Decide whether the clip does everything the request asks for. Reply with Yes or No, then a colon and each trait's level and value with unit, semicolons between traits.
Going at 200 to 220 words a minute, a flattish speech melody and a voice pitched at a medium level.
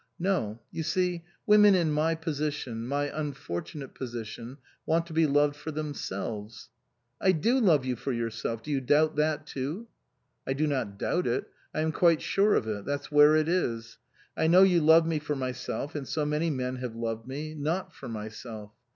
No: fast, 205 wpm; average, 4.9 semitones; medium, 145 Hz